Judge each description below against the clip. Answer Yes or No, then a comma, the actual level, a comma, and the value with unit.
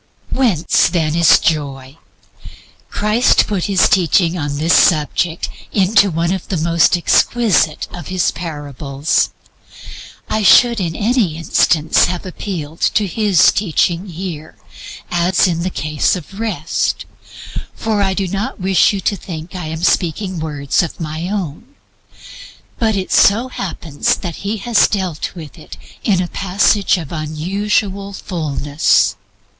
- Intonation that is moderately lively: Yes, average, 4.1 semitones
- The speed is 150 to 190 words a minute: No, slow, 135 wpm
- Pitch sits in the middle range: Yes, medium, 180 Hz